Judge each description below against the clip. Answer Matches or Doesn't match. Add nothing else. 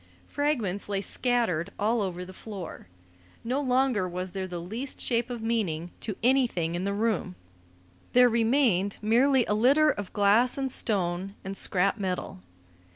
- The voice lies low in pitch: Doesn't match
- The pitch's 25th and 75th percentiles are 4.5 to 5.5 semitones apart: Matches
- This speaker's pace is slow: Doesn't match